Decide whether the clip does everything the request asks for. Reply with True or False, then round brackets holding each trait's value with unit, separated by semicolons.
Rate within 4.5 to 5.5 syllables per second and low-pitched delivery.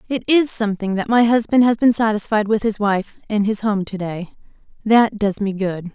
False (5.1 syllables/s; 210 Hz)